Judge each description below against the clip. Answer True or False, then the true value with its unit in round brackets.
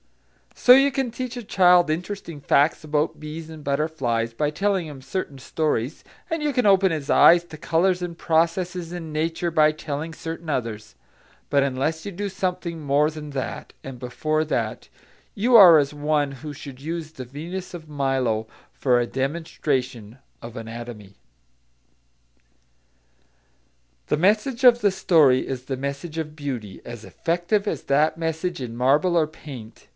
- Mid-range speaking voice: True (155 Hz)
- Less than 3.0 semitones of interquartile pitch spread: False (4.3 semitones)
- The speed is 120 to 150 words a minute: False (160 wpm)